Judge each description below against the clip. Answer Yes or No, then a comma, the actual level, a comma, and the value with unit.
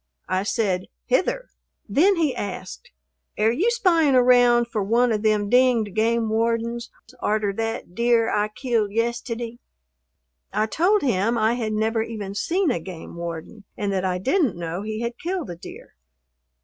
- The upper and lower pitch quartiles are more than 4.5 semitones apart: No, average, 3.1 semitones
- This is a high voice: Yes, high, 225 Hz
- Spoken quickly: No, average, 160 wpm